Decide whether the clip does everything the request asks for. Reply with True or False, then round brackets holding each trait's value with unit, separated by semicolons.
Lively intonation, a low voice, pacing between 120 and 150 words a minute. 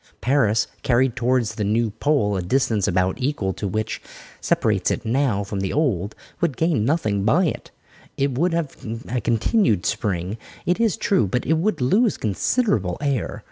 False (6.4 semitones; 120 Hz; 180 wpm)